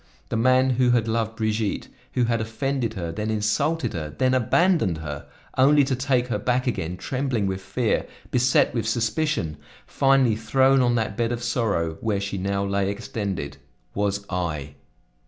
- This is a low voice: Yes, low, 115 Hz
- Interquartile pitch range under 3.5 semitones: No, average, 4.4 semitones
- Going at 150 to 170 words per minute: Yes, average, 165 wpm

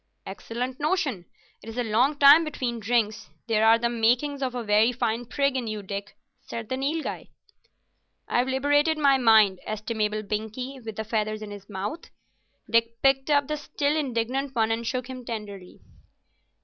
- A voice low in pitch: No, high, 235 Hz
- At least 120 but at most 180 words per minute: Yes, average, 170 wpm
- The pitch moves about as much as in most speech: Yes, average, 3.9 semitones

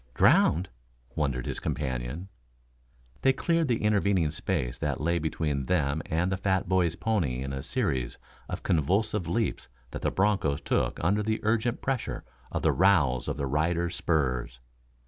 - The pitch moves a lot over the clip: Yes, wide, 6.3 semitones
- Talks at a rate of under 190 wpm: Yes, average, 155 wpm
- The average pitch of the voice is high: No, very low, 85 Hz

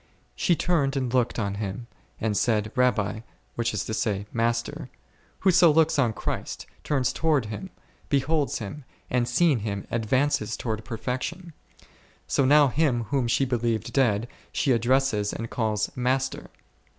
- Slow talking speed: No, average, 145 wpm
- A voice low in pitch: Yes, low, 125 Hz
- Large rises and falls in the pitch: No, average, 4.0 semitones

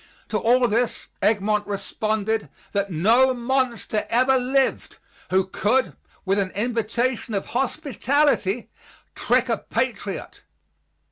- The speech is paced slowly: Yes, slow, 110 wpm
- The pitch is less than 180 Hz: No, high, 230 Hz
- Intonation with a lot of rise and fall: No, average, 3.8 semitones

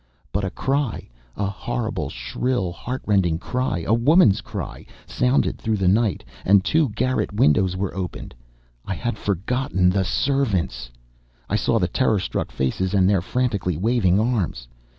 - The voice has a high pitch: No, low, 100 Hz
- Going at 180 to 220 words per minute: No, average, 145 wpm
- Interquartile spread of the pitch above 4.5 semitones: Yes, average, 4.9 semitones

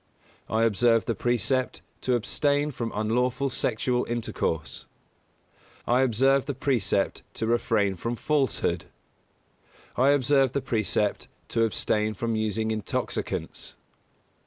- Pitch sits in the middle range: No, low, 120 Hz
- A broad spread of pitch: No, average, 3.1 semitones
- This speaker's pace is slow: Yes, slow, 110 wpm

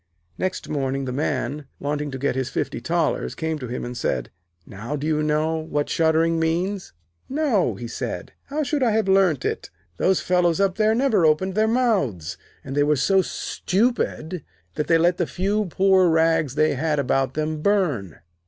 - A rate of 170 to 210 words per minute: Yes, average, 180 wpm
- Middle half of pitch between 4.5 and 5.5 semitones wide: Yes, average, 5.1 semitones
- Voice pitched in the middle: Yes, medium, 160 Hz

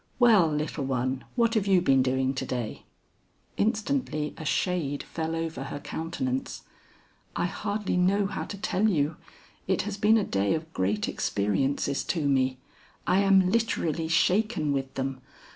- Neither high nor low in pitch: Yes, medium, 160 Hz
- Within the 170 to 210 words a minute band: No, average, 155 wpm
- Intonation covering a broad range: Yes, wide, 6.7 semitones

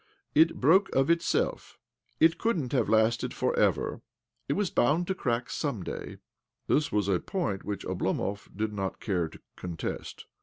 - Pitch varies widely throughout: Yes, wide, 8.2 semitones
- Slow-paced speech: No, average, 165 wpm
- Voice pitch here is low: Yes, low, 120 Hz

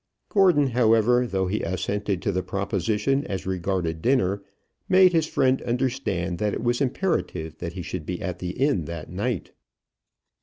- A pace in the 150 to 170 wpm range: Yes, average, 160 wpm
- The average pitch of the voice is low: Yes, low, 100 Hz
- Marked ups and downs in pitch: Yes, wide, 5.8 semitones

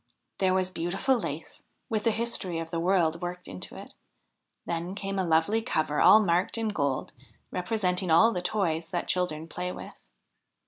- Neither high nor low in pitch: Yes, medium, 180 Hz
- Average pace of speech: Yes, average, 170 wpm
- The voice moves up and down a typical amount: Yes, average, 3.2 semitones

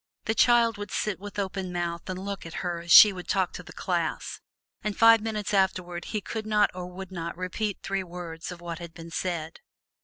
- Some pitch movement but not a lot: Yes, average, 3.0 semitones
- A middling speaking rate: No, fast, 215 wpm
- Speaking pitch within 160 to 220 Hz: Yes, medium, 185 Hz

